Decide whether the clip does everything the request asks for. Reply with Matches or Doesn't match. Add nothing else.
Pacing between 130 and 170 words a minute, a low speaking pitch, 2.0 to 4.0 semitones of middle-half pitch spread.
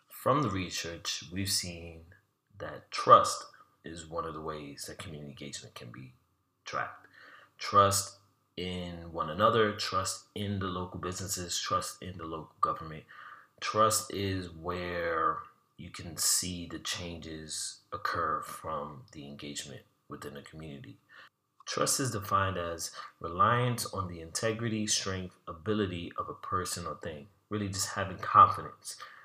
Matches